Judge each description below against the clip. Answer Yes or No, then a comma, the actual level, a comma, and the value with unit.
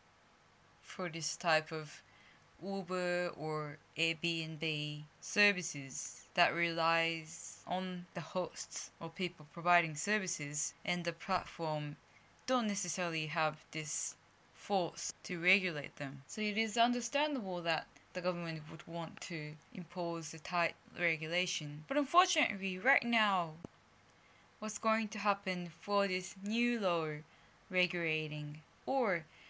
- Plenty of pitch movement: No, average, 3.4 semitones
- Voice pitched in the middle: Yes, medium, 175 Hz